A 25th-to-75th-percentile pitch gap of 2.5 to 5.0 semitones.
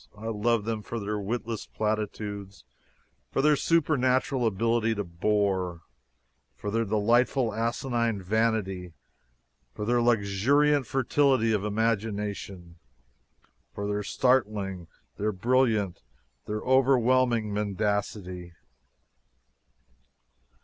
Yes: average, 2.9 semitones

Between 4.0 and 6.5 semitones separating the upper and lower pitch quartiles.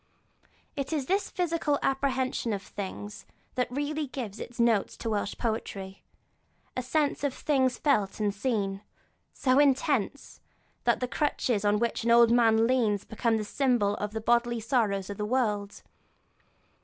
Yes: average, 4.3 semitones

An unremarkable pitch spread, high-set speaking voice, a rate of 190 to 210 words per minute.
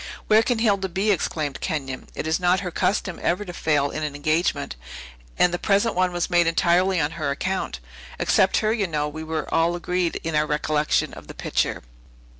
No: average, 3.6 semitones; medium, 170 Hz; average, 200 wpm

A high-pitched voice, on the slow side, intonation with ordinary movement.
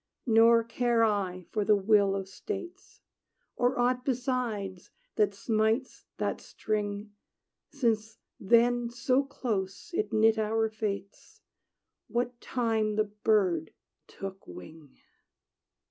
Yes: high, 220 Hz; slow, 110 wpm; average, 3.0 semitones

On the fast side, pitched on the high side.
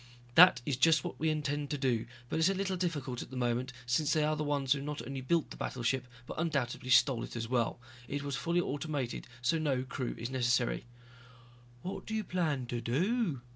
No: fast, 215 wpm; medium, 140 Hz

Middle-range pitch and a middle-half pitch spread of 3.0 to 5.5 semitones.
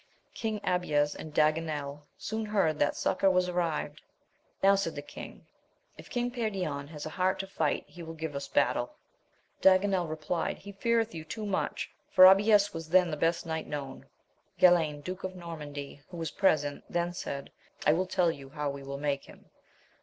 Yes: medium, 165 Hz; average, 4.1 semitones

